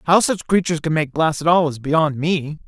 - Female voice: No, male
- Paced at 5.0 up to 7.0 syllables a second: Yes, 5.3 syllables/s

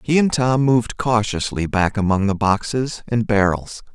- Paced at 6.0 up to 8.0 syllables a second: No, 4.6 syllables/s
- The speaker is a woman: No, male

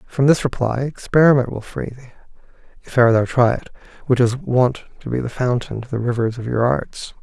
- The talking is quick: Yes, fast, 210 wpm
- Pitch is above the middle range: No, low, 125 Hz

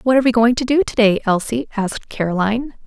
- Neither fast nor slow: No, fast, 230 wpm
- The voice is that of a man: No, female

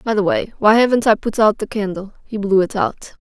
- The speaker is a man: No, female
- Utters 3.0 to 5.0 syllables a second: No, 5.5 syllables/s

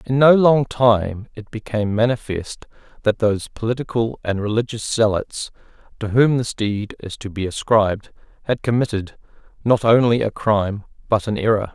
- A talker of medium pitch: No, low, 110 Hz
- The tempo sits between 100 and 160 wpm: Yes, average, 155 wpm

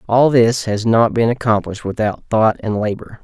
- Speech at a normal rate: Yes, average, 185 wpm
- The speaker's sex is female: No, male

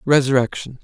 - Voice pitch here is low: Yes, low, 130 Hz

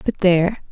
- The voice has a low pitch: No, medium, 185 Hz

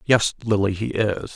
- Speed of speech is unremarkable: Yes, average, 180 wpm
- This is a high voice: No, low, 105 Hz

